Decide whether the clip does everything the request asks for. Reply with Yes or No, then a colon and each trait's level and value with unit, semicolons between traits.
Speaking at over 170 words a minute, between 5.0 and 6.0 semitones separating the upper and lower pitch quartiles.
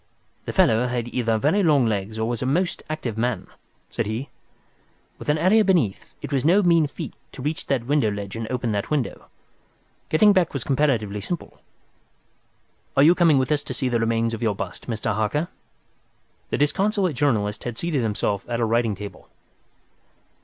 Yes: average, 180 wpm; wide, 5.4 semitones